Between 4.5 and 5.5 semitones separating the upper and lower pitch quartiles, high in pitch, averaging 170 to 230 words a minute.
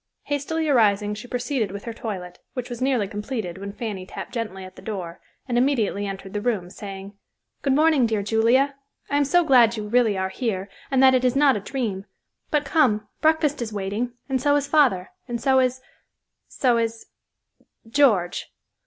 Yes: average, 4.8 semitones; high, 230 Hz; average, 180 wpm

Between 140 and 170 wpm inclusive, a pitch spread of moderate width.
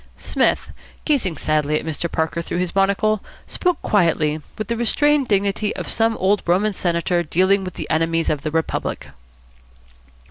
Yes: average, 155 wpm; average, 4.6 semitones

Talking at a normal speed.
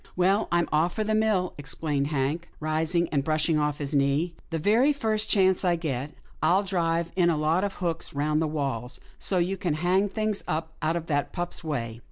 No: fast, 210 wpm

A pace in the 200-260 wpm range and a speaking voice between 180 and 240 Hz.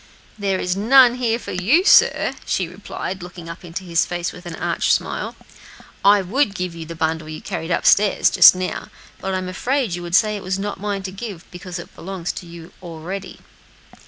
Yes: fast, 205 wpm; medium, 185 Hz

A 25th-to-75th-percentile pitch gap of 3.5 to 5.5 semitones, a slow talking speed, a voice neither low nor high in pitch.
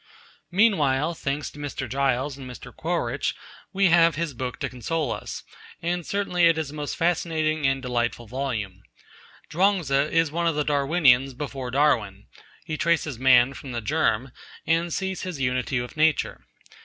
No: average, 4.3 semitones; average, 165 wpm; medium, 145 Hz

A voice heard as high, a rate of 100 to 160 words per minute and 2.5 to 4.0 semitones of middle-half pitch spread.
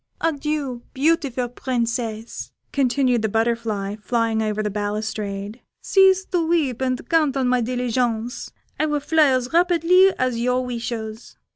No: very high, 250 Hz; slow, 135 wpm; average, 4.6 semitones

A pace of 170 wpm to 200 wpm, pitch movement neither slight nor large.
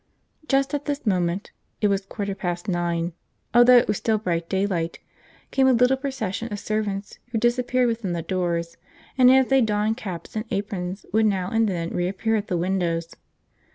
Yes: average, 180 wpm; average, 4.9 semitones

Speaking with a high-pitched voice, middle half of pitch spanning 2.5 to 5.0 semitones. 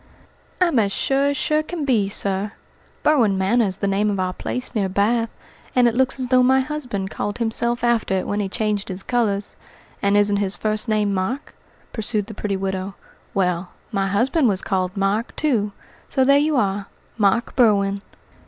Yes: high, 210 Hz; average, 4.0 semitones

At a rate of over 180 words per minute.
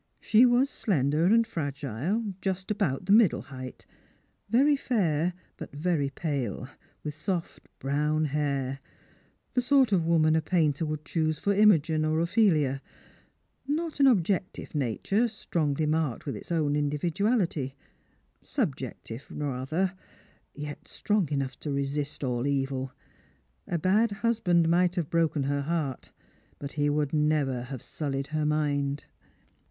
No: slow, 135 wpm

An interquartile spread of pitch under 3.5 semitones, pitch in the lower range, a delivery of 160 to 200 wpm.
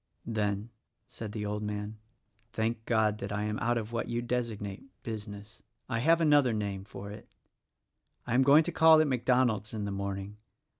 Yes: average, 2.7 semitones; low, 110 Hz; average, 180 wpm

